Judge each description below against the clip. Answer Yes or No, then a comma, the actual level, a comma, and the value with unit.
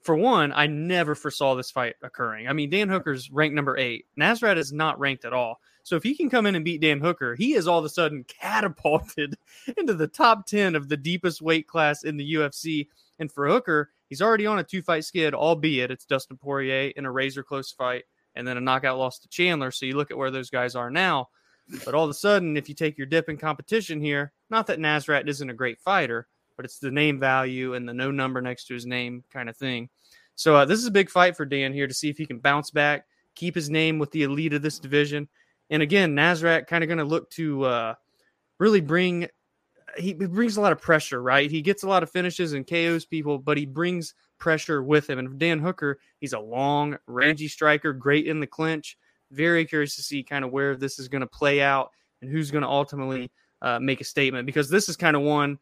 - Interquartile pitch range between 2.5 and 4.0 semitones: Yes, average, 3.4 semitones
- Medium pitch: Yes, medium, 150 Hz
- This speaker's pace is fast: Yes, fast, 240 wpm